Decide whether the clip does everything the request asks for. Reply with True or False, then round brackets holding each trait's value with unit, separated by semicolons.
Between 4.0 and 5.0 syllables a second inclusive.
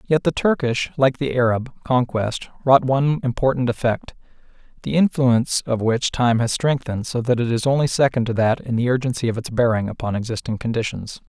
False (5.6 syllables/s)